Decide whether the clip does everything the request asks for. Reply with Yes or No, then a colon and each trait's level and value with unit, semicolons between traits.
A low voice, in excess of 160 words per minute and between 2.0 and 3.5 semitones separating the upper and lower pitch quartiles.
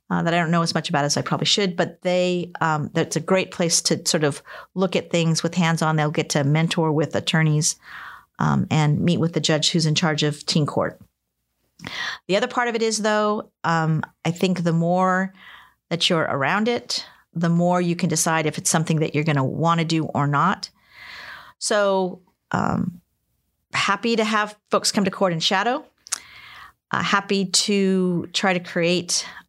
No: medium, 170 Hz; average, 195 wpm; average, 3.2 semitones